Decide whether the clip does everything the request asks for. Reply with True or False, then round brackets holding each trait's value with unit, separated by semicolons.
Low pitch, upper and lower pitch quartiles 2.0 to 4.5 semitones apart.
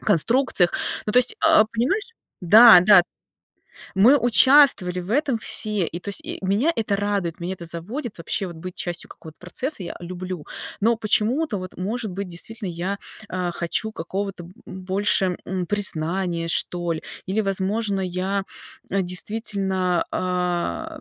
False (190 Hz; 3.5 semitones)